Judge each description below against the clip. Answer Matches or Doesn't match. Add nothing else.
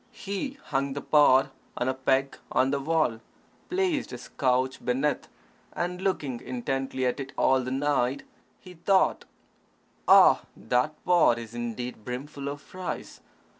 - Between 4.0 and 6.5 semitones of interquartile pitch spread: Doesn't match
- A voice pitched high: Doesn't match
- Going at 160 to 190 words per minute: Doesn't match